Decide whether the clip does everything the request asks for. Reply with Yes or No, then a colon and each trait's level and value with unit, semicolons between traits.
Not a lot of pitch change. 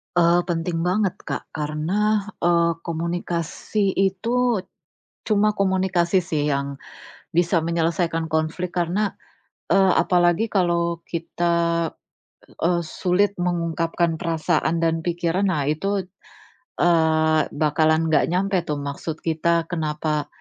Yes: narrow, 2.1 semitones